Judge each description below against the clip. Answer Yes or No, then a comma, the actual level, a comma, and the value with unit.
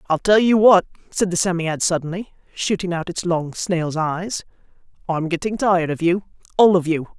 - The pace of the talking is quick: No, average, 185 wpm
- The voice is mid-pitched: Yes, medium, 175 Hz